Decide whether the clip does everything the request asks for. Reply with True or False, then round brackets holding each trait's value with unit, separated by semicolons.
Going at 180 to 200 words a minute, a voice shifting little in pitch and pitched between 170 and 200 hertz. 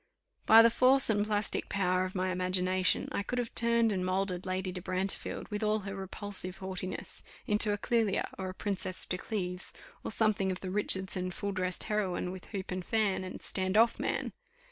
True (190 wpm; 2.2 semitones; 190 Hz)